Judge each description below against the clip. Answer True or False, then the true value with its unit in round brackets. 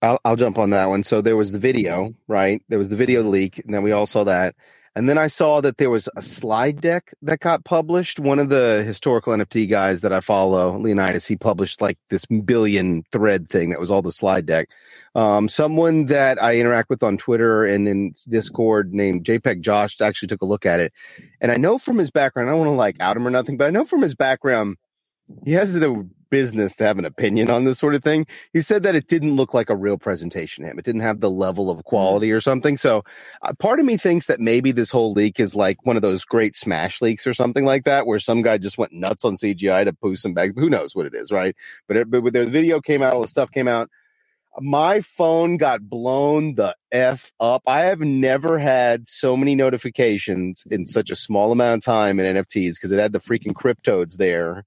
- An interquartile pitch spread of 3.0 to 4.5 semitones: False (5.2 semitones)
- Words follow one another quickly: True (240 wpm)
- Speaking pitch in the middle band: False (115 Hz)